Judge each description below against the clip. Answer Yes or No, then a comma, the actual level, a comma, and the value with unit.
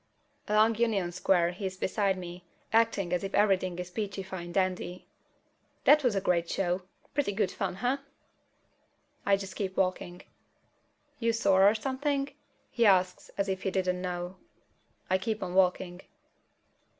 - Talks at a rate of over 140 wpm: Yes, average, 150 wpm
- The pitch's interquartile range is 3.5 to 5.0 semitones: No, average, 2.7 semitones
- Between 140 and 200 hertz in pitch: Yes, high, 190 Hz